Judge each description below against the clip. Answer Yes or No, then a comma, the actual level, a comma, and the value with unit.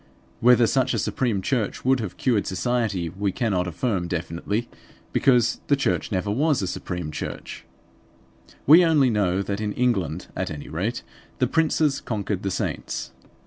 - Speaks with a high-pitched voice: No, low, 105 Hz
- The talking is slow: No, average, 155 wpm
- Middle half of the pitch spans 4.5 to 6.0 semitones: Yes, average, 5.2 semitones